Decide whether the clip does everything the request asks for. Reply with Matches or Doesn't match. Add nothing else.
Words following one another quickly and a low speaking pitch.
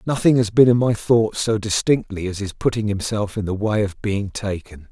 Matches